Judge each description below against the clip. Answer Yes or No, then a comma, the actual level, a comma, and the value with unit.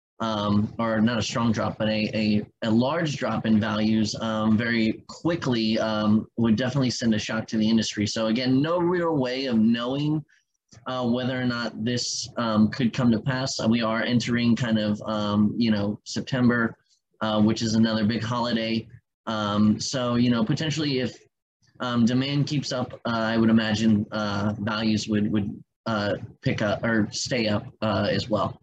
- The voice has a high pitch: No, low, 115 Hz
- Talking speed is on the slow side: No, average, 180 wpm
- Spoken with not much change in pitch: Yes, narrow, 2.3 semitones